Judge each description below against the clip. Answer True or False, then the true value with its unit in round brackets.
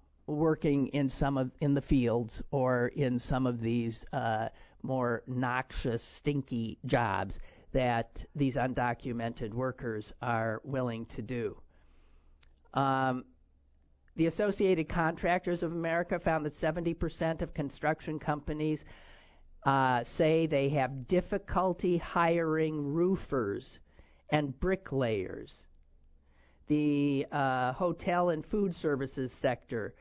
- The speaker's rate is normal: False (105 wpm)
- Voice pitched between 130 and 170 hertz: True (135 Hz)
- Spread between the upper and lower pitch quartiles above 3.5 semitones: True (5.3 semitones)